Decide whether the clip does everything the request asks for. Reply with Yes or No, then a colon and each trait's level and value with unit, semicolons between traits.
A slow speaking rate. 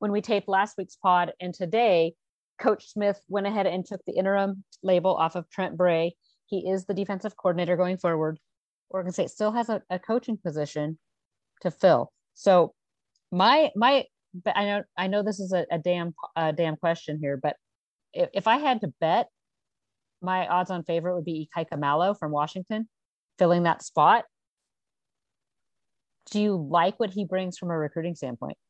No: average, 175 wpm